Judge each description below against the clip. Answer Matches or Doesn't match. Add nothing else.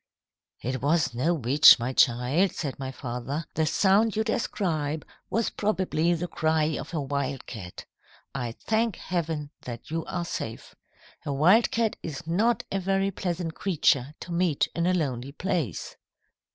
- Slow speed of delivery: Doesn't match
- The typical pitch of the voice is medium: Matches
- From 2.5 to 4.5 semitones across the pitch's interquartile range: Doesn't match